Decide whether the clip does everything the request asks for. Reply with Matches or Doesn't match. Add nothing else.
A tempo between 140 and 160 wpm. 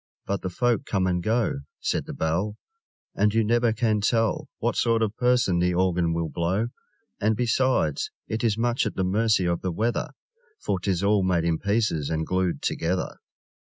Doesn't match